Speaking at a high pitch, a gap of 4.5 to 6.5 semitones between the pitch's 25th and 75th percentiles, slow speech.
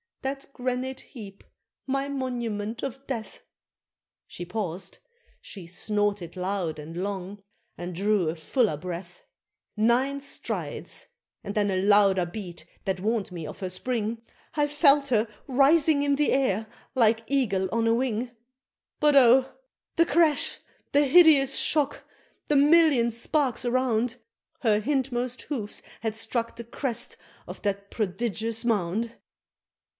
Yes: high, 230 Hz; average, 5.2 semitones; slow, 130 wpm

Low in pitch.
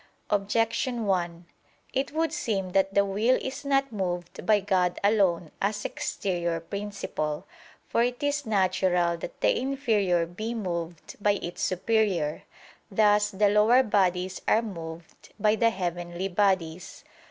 No: high, 195 Hz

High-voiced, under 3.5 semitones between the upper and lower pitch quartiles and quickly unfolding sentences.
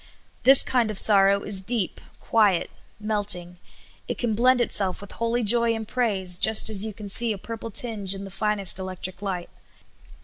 No: high, 210 Hz; average, 2.9 semitones; average, 175 wpm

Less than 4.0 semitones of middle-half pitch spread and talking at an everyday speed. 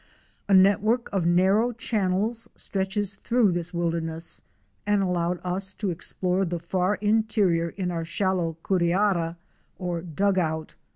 No: average, 2.9 semitones; slow, 130 wpm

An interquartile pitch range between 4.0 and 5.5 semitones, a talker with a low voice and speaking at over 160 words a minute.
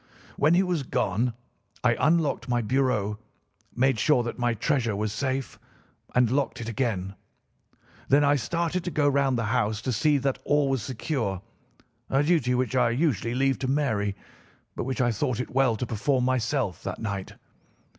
No: average, 3.6 semitones; low, 125 Hz; average, 170 wpm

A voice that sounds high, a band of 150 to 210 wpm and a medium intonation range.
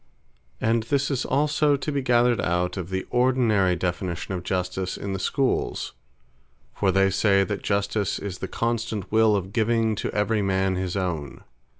No: low, 100 Hz; average, 170 wpm; average, 3.9 semitones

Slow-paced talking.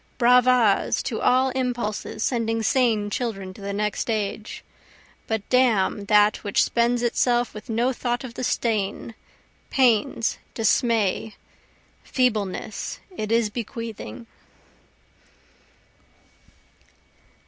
Yes: slow, 100 wpm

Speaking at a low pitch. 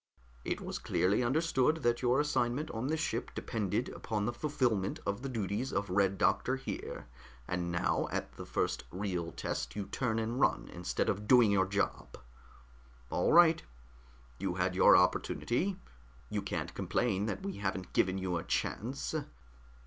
Yes: low, 110 Hz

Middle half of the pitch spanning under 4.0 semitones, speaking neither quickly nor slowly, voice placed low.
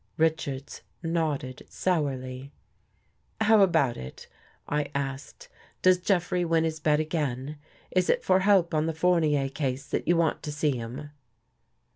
No: average, 3.6 semitones; average, 155 wpm; medium, 155 Hz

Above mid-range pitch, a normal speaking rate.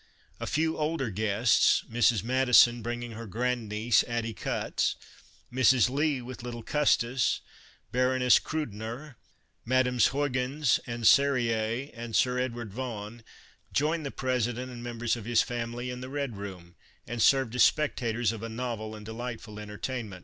No: low, 120 Hz; average, 150 wpm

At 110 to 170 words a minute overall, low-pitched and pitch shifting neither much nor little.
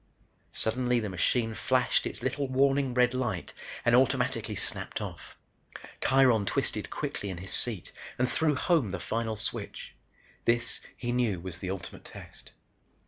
Yes: average, 145 wpm; low, 120 Hz; average, 4.0 semitones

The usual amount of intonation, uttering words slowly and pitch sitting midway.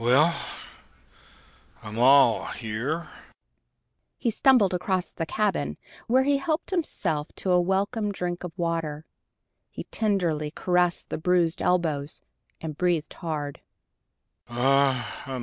Yes: average, 4.3 semitones; slow, 110 wpm; medium, 175 Hz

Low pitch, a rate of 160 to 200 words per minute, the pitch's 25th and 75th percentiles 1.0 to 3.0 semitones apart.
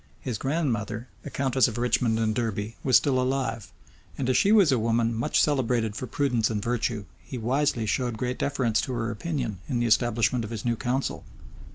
Yes: low, 120 Hz; average, 195 wpm; average, 2.7 semitones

